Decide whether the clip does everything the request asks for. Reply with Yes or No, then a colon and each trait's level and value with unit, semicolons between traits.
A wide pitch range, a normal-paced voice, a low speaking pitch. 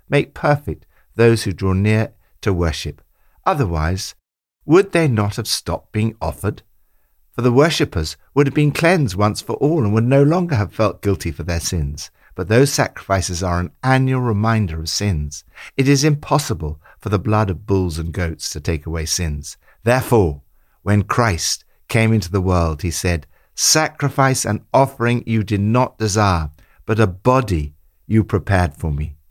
Yes: wide, 6.5 semitones; average, 170 wpm; low, 105 Hz